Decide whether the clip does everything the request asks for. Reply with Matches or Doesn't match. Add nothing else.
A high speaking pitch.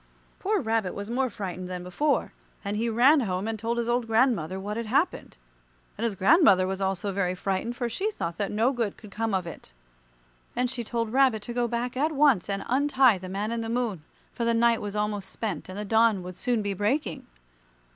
Matches